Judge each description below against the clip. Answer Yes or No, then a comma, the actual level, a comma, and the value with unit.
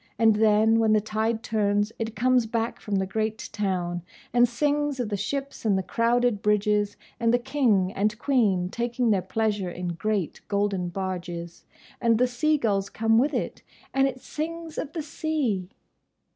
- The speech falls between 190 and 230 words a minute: No, average, 170 wpm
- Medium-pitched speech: No, high, 220 Hz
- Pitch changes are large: No, average, 3.4 semitones